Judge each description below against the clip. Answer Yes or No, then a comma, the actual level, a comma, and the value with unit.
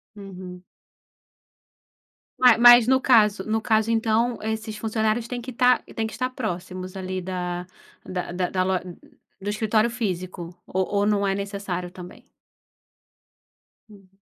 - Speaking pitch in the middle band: No, high, 205 Hz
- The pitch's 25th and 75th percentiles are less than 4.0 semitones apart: Yes, average, 3.3 semitones